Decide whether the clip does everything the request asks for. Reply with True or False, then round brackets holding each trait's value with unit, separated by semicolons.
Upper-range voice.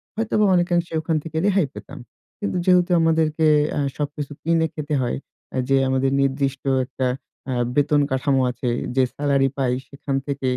False (145 Hz)